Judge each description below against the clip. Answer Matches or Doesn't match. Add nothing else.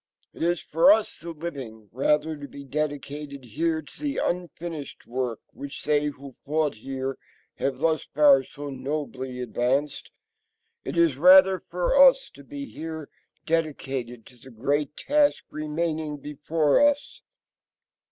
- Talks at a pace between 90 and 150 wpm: Matches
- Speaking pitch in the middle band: Matches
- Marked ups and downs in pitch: Doesn't match